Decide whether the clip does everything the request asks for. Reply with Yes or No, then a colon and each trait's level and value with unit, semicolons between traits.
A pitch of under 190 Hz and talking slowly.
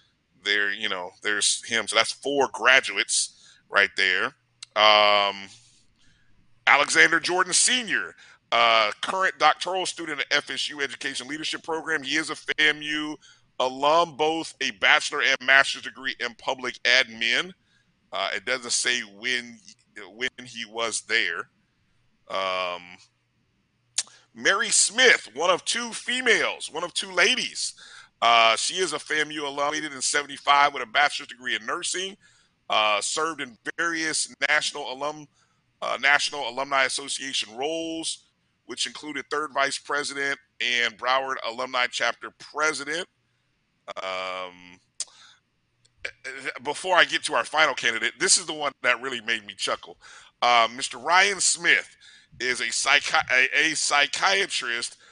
Yes: medium, 140 Hz; slow, 130 wpm